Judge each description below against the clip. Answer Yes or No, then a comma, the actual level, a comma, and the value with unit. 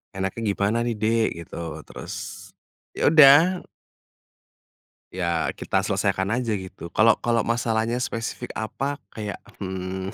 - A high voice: No, low, 110 Hz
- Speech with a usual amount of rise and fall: Yes, average, 3.8 semitones